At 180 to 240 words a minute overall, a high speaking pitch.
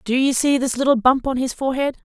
No: fast, 255 wpm; very high, 260 Hz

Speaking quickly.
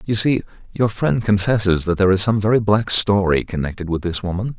Yes: fast, 210 wpm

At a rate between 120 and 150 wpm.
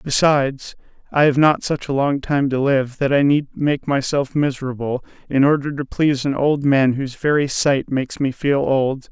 No: average, 195 wpm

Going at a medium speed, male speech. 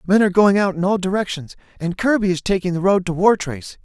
No: fast, 235 wpm; male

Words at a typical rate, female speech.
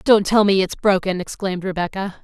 Yes: average, 190 wpm; female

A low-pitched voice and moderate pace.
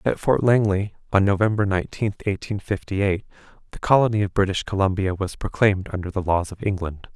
Yes: low, 100 Hz; average, 175 wpm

